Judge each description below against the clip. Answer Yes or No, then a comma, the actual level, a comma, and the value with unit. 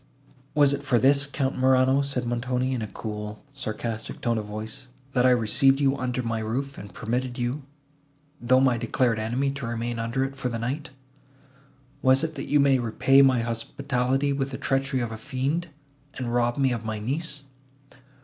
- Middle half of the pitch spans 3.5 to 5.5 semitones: No, average, 2.8 semitones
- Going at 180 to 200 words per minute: Yes, average, 185 wpm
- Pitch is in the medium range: No, low, 130 Hz